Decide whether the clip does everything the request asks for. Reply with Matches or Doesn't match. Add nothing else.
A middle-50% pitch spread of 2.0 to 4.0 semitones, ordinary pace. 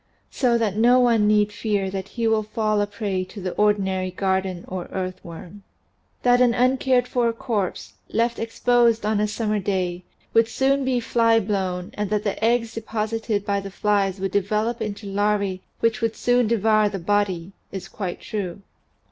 Matches